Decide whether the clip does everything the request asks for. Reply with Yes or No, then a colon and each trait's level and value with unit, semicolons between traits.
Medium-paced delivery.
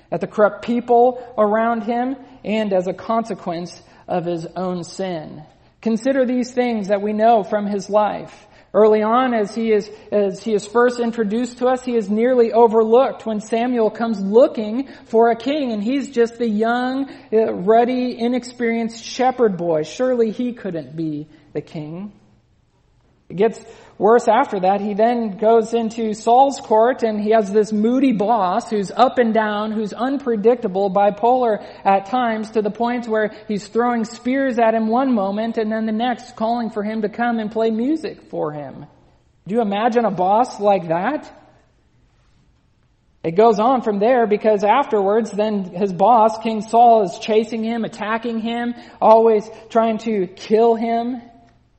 Yes: average, 165 wpm